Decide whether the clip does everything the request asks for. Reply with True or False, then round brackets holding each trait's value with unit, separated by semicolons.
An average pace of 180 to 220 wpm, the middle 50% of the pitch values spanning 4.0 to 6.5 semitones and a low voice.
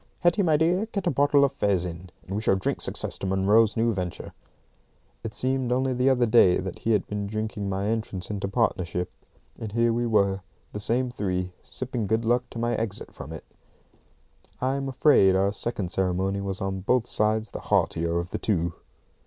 True (195 wpm; 4.3 semitones; 105 Hz)